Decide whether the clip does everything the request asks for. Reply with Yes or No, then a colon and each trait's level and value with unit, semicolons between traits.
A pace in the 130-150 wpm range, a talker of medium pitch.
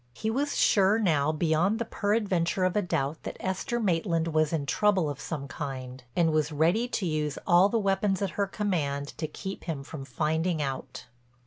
No: average, 195 wpm; medium, 170 Hz